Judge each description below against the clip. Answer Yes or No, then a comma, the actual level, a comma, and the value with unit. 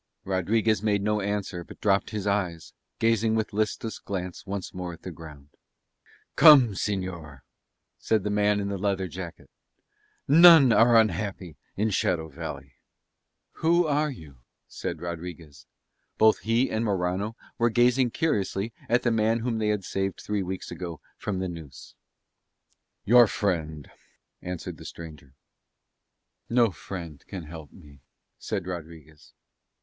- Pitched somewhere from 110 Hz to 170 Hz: No, low, 100 Hz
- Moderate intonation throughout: Yes, average, 4.5 semitones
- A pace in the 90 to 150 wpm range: Yes, average, 140 wpm